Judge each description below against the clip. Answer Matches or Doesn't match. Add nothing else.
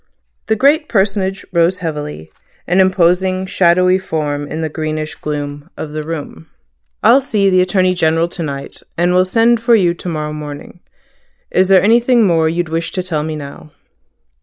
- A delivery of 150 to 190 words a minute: Matches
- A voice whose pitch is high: Doesn't match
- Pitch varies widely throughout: Doesn't match